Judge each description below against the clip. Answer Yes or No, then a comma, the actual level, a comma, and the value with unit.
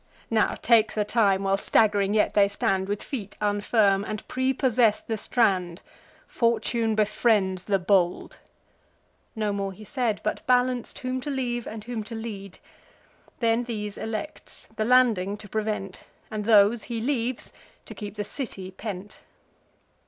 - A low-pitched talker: No, high, 215 Hz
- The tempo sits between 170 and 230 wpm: No, average, 145 wpm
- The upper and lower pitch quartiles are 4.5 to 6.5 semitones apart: No, average, 2.7 semitones